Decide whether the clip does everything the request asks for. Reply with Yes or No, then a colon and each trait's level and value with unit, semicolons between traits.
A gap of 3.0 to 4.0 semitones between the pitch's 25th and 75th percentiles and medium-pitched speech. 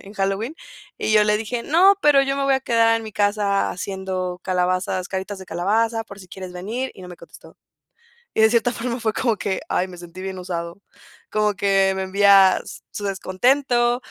No: average, 3.5 semitones; high, 200 Hz